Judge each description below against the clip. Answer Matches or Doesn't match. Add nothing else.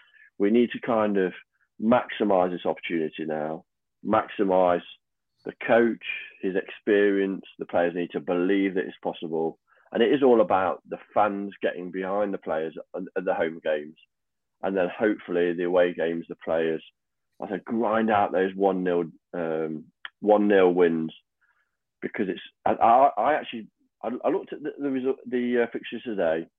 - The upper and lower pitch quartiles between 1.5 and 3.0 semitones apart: Doesn't match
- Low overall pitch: Matches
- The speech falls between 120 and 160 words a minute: Matches